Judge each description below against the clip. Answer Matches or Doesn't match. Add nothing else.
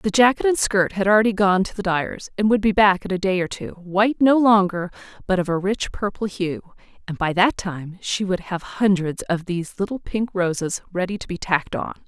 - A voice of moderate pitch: Doesn't match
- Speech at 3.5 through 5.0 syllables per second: Doesn't match